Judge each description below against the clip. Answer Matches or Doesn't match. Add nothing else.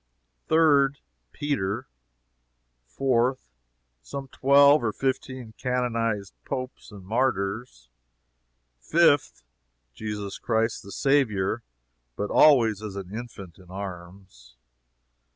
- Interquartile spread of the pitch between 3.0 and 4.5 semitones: Doesn't match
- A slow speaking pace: Matches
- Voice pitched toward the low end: Matches